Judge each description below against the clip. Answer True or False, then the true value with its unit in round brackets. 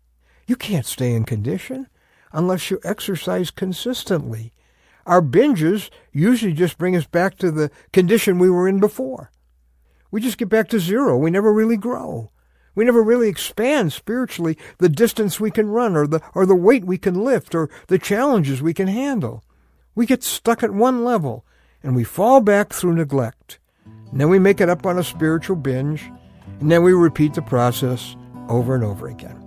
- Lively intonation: True (8.6 semitones)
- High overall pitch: False (180 Hz)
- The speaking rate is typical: True (180 wpm)